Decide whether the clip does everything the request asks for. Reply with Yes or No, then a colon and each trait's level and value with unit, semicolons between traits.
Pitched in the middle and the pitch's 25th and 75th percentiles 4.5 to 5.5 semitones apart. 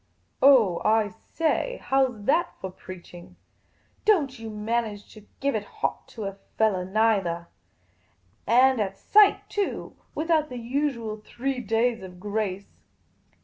No: high, 225 Hz; average, 5.0 semitones